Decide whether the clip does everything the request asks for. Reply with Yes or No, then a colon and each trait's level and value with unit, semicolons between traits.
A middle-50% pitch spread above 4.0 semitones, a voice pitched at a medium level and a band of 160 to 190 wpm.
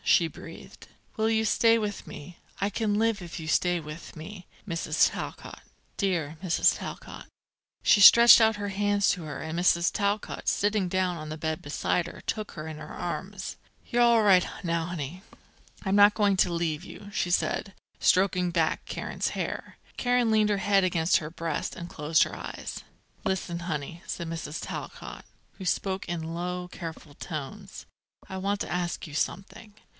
No: average, 3.6 semitones; medium, 180 Hz; average, 175 wpm